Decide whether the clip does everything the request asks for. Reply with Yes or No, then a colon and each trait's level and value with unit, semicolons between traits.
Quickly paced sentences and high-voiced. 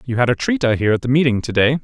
No: fast, 360 wpm; low, 130 Hz